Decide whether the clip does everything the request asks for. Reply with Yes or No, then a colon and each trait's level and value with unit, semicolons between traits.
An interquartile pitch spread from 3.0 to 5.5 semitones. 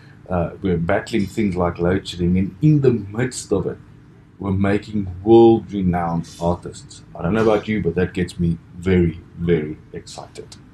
Yes: average, 3.6 semitones